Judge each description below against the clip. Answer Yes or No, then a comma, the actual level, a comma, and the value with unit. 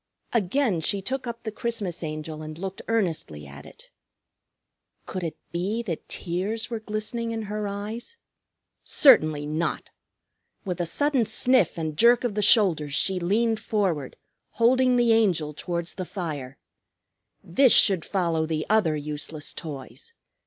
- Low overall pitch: No, high, 190 Hz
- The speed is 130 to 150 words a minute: Yes, average, 145 wpm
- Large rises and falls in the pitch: Yes, wide, 6.2 semitones